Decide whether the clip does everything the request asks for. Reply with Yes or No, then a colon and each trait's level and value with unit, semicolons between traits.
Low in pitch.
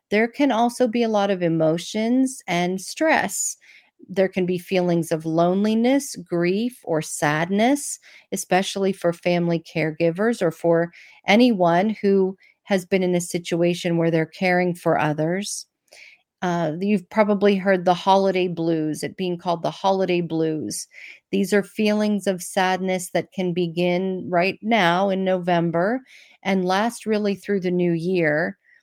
No: medium, 185 Hz